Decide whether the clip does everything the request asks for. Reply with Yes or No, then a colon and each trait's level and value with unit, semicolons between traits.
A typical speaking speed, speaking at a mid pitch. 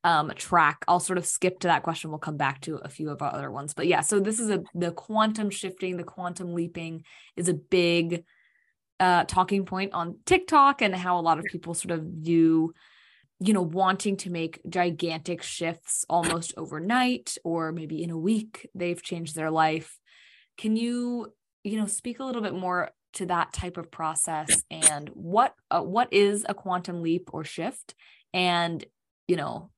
Yes: average, 185 wpm; medium, 175 Hz